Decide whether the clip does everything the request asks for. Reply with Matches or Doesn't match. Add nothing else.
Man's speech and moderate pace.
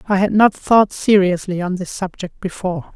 Doesn't match